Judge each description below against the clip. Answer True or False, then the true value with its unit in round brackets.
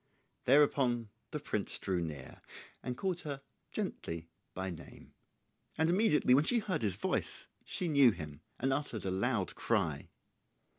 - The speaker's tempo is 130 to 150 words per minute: True (145 wpm)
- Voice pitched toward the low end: True (125 Hz)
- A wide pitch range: True (8.1 semitones)